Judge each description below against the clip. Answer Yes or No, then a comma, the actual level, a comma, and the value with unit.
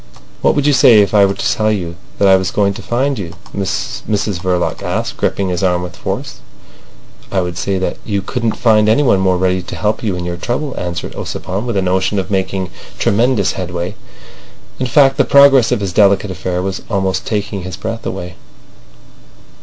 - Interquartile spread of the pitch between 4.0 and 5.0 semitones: No, average, 2.9 semitones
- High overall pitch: No, low, 100 Hz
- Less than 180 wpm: No, average, 195 wpm